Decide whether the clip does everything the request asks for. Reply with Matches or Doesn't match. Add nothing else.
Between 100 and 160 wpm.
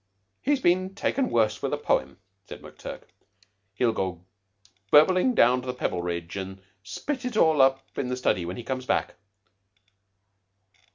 Matches